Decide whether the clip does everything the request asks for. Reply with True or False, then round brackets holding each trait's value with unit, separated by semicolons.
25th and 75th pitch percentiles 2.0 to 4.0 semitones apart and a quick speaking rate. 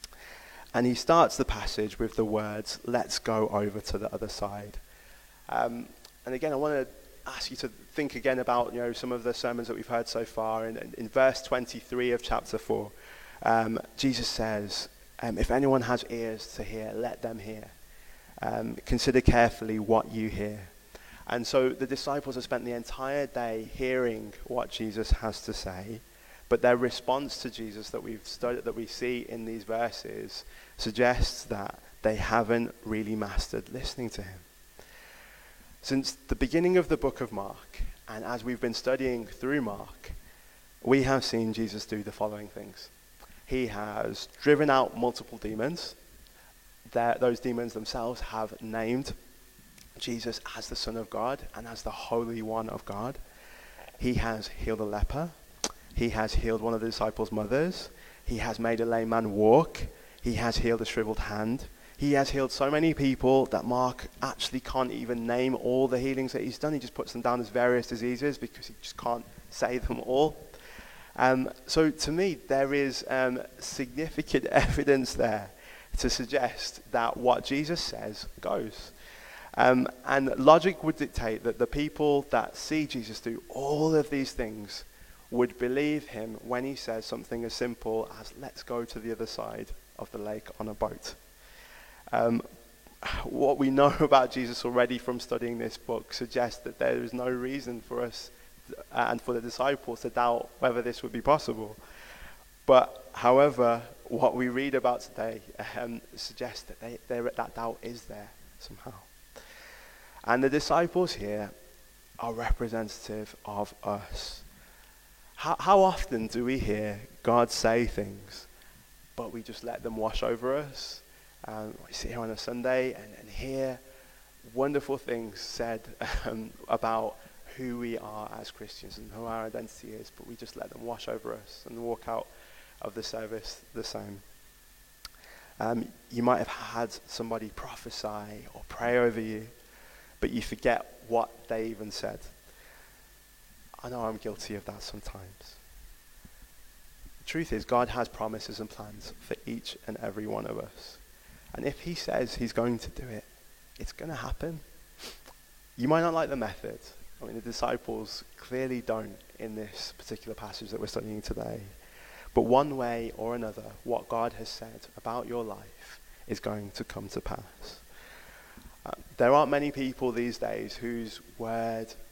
False (2.7 semitones; 165 wpm)